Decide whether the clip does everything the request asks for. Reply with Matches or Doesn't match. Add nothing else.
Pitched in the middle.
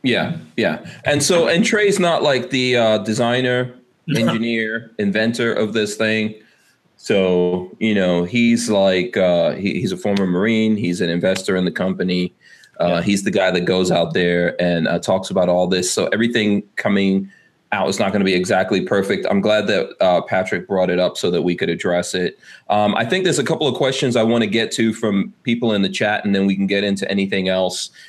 Doesn't match